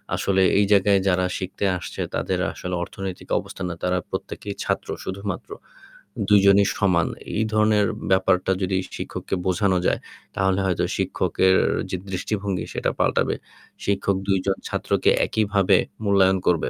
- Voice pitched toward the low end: Yes, very low, 95 Hz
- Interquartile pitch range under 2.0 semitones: Yes, narrow, 1.3 semitones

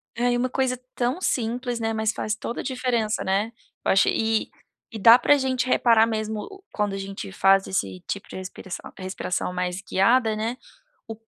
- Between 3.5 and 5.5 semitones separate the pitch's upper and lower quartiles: Yes, average, 3.9 semitones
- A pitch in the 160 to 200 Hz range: No, high, 220 Hz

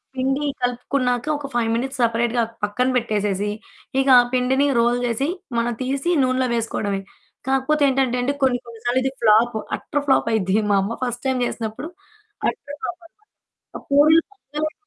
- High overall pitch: Yes, very high, 250 Hz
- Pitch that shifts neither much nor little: Yes, average, 3.0 semitones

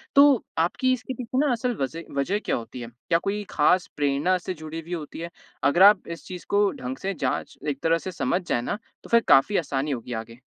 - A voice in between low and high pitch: Yes, medium, 170 Hz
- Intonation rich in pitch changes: Yes, wide, 6.5 semitones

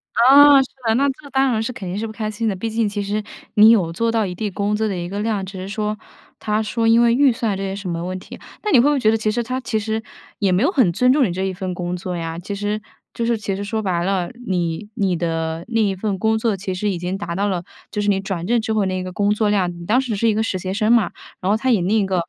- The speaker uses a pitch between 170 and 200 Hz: No, high, 210 Hz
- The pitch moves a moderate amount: Yes, average, 3.3 semitones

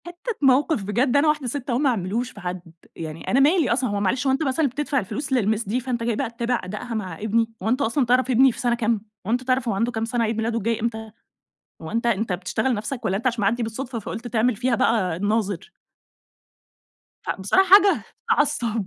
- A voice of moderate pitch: No, high, 235 Hz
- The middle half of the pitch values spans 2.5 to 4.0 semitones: Yes, average, 3.3 semitones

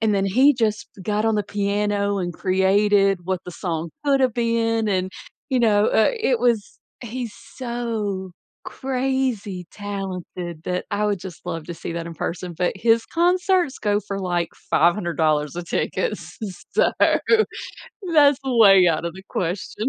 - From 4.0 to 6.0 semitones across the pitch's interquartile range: Yes, average, 4.3 semitones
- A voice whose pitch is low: No, high, 205 Hz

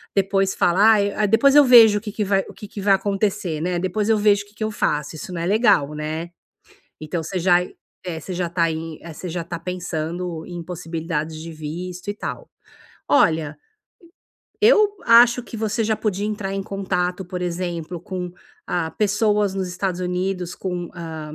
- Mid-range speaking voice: Yes, medium, 180 Hz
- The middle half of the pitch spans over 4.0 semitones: No, average, 3.5 semitones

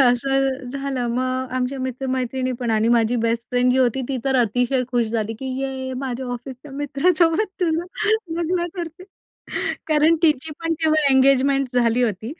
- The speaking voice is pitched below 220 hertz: No, very high, 260 Hz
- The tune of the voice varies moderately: No, narrow, 2.3 semitones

